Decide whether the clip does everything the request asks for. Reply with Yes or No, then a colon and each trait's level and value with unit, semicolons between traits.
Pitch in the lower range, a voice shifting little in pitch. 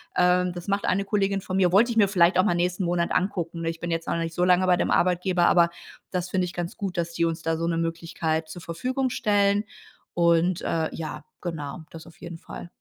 No: medium, 175 Hz; narrow, 2.0 semitones